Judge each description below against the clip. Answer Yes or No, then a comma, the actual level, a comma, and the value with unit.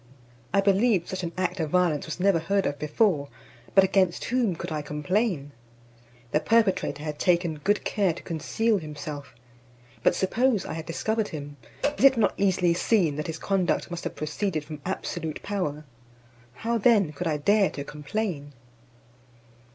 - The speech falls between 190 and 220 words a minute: No, average, 165 wpm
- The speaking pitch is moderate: Yes, medium, 175 Hz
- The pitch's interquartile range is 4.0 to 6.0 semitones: Yes, average, 4.8 semitones